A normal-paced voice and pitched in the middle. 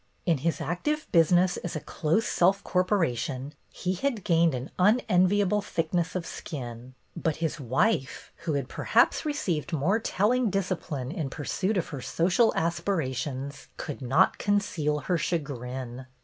Yes: average, 145 wpm; medium, 170 Hz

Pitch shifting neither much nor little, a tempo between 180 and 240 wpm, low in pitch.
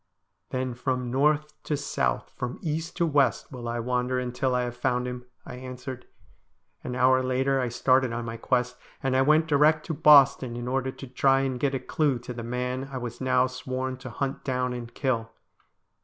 No: narrow, 1.5 semitones; average, 200 wpm; low, 130 Hz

